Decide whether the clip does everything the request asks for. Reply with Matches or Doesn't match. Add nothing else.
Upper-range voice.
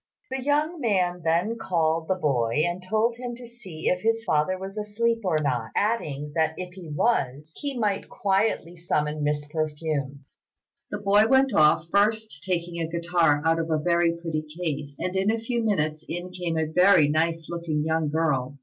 Doesn't match